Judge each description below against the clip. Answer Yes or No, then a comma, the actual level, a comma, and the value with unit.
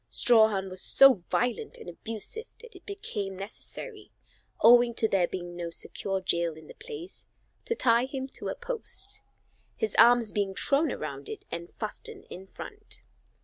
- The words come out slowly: No, average, 160 wpm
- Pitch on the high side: Yes, high, 235 Hz